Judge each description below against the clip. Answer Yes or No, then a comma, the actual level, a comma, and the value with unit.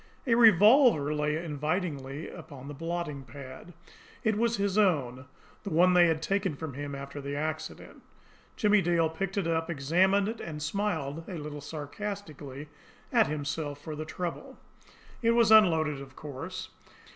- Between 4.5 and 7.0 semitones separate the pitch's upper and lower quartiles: Yes, average, 5.2 semitones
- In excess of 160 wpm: No, average, 155 wpm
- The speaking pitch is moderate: Yes, medium, 160 Hz